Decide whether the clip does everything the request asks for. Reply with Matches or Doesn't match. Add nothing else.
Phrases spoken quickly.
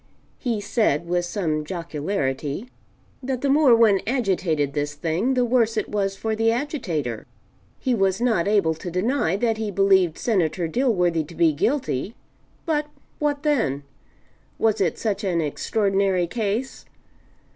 Doesn't match